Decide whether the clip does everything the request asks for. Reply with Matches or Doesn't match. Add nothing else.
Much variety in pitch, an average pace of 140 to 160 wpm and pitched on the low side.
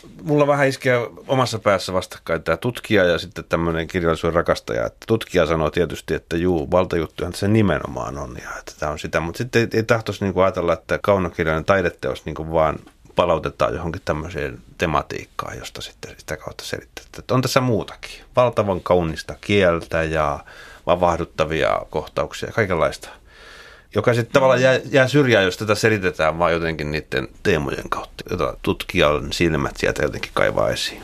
Matches